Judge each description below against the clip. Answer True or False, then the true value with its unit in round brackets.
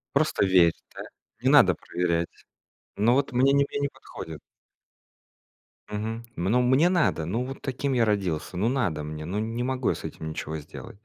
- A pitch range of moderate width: False (7.2 semitones)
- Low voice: True (110 Hz)